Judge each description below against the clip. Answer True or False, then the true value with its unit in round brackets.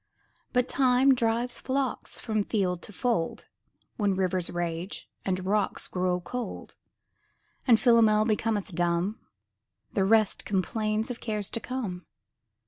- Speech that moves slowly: True (125 wpm)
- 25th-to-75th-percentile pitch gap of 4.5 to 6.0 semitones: False (4.1 semitones)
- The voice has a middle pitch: False (215 Hz)